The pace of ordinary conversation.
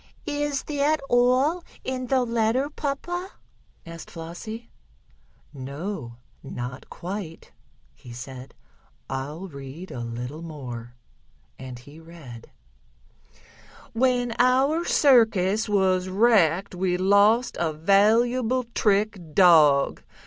No: slow, 100 wpm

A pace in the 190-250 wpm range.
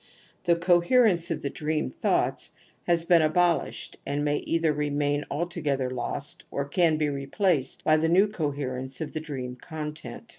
No: average, 160 wpm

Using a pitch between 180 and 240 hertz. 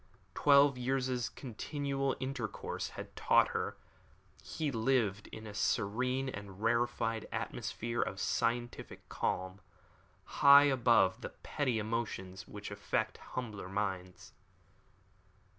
No: low, 115 Hz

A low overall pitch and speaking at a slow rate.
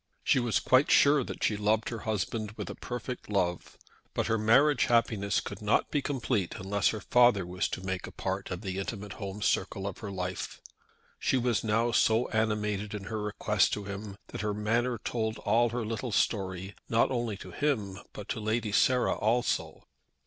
No: low, 110 Hz; average, 190 wpm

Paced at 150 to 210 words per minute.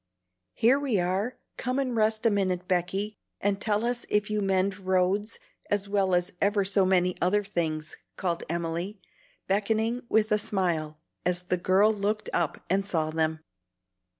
Yes: average, 160 wpm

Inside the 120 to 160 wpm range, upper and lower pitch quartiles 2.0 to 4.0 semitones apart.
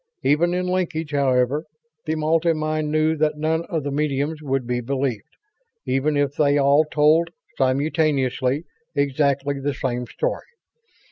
Yes: average, 140 wpm; narrow, 2.4 semitones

